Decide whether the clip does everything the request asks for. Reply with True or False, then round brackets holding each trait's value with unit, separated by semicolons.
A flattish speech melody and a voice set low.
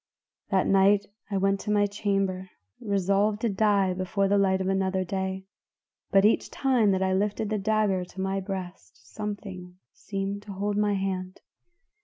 False (1.4 semitones; 195 Hz)